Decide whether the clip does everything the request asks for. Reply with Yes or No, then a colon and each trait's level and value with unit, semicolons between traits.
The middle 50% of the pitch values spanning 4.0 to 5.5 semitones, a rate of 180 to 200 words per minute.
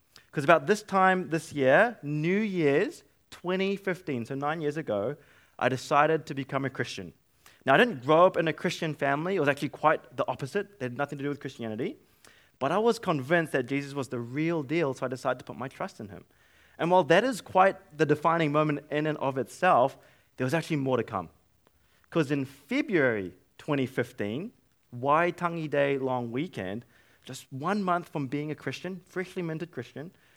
Yes: average, 4.8 semitones; average, 190 wpm